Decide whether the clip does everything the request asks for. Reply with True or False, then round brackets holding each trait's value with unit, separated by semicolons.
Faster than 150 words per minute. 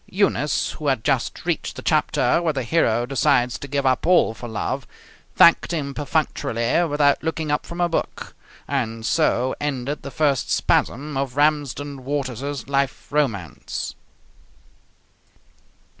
False (140 wpm)